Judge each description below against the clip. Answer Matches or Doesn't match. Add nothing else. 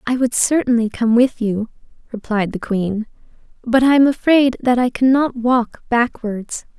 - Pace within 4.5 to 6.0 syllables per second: Doesn't match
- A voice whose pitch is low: Doesn't match